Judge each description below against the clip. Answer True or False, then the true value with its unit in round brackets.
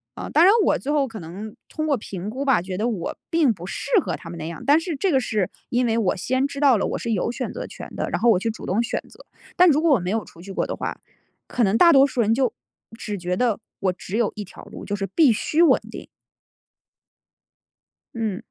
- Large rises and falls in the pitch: True (5.9 semitones)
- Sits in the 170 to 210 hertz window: False (225 Hz)